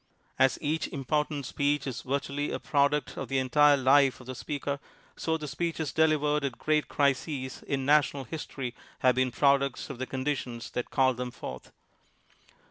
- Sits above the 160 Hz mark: No, medium, 140 Hz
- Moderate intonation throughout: No, narrow, 2.2 semitones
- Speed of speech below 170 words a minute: No, average, 180 wpm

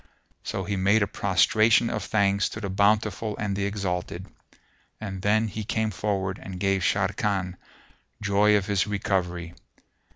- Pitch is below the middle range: Yes, low, 100 Hz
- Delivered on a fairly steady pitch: Yes, narrow, 1.8 semitones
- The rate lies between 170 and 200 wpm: No, average, 150 wpm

